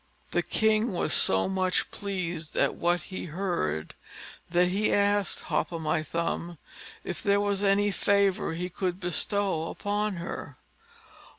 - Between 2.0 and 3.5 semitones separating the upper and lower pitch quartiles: Yes, average, 2.9 semitones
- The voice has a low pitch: No, medium, 185 Hz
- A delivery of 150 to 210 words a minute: No, average, 140 wpm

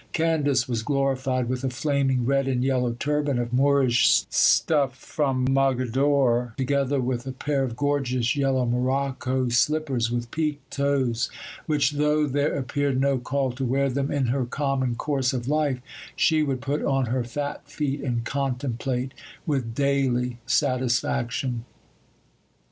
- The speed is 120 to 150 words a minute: Yes, average, 145 wpm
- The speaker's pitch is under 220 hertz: Yes, low, 135 Hz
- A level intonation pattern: Yes, narrow, 2.2 semitones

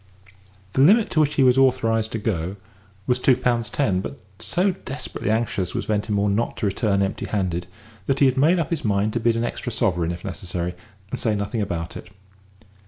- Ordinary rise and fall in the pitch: Yes, average, 4.9 semitones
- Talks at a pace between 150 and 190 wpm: No, average, 200 wpm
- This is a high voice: No, low, 110 Hz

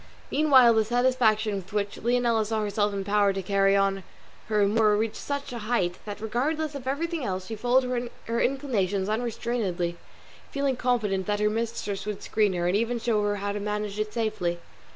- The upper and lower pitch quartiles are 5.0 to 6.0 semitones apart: No, average, 3.2 semitones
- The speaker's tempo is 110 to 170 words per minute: No, average, 180 wpm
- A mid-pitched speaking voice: No, high, 215 Hz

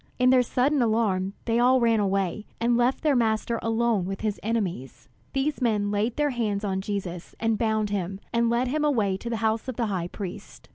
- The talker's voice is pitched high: Yes, high, 225 Hz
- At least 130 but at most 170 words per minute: No, fast, 205 wpm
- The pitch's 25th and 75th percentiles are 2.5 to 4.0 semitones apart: Yes, average, 3.2 semitones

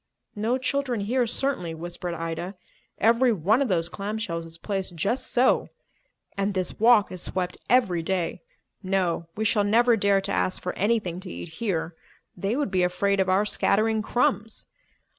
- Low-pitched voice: No, high, 200 Hz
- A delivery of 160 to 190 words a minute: Yes, average, 170 wpm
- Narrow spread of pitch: No, average, 4.1 semitones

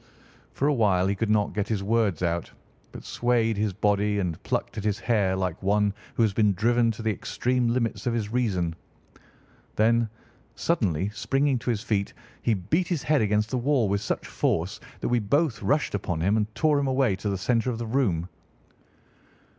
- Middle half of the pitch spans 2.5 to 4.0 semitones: Yes, average, 3.4 semitones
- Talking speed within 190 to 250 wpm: Yes, average, 195 wpm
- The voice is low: Yes, low, 110 Hz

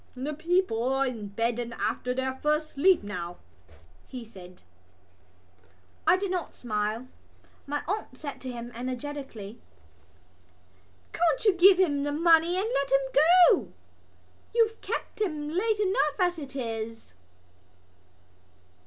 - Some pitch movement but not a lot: No, wide, 6.5 semitones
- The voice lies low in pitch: No, very high, 280 Hz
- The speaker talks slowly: Yes, slow, 130 wpm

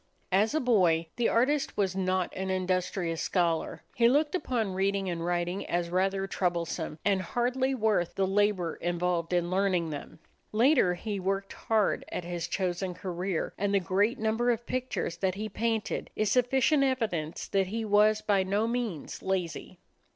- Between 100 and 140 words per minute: No, average, 165 wpm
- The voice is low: No, high, 195 Hz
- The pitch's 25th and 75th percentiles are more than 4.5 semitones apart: No, average, 3.8 semitones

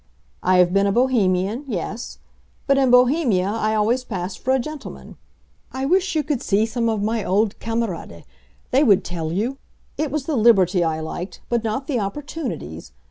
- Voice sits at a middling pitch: No, high, 225 Hz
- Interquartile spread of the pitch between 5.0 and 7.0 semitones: Yes, wide, 5.5 semitones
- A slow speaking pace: No, average, 170 wpm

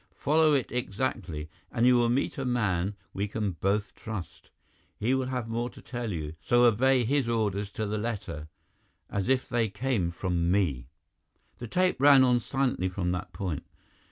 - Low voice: Yes, low, 110 Hz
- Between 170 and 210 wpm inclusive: Yes, average, 175 wpm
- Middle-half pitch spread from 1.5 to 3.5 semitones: No, average, 5.1 semitones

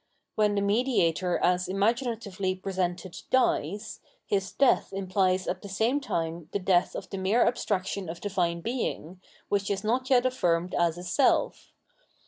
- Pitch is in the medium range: No, high, 195 Hz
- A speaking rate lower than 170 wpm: Yes, average, 150 wpm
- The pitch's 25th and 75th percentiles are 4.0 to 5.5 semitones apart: No, average, 3.5 semitones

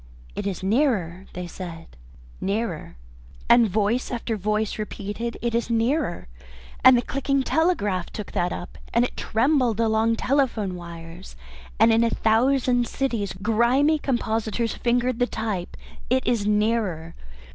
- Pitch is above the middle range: Yes, high, 225 Hz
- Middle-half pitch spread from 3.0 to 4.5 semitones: Yes, average, 3.5 semitones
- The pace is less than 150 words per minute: Yes, slow, 135 wpm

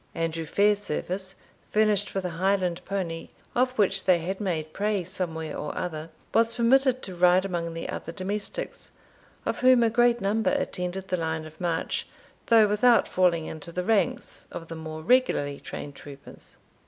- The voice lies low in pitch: No, medium, 185 Hz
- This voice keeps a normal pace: Yes, average, 165 wpm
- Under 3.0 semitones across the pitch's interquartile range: No, average, 4.4 semitones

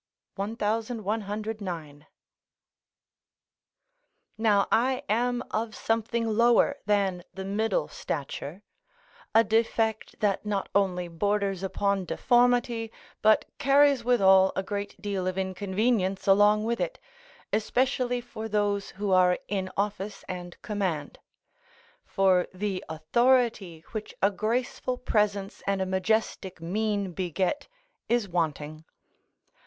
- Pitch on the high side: Yes, high, 205 Hz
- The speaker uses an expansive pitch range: No, average, 3.1 semitones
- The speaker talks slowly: Yes, slow, 105 wpm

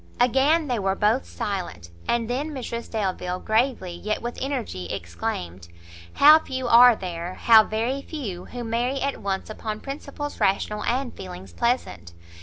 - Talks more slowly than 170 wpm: Yes, average, 150 wpm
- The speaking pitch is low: No, high, 225 Hz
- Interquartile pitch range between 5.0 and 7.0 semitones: Yes, wide, 5.6 semitones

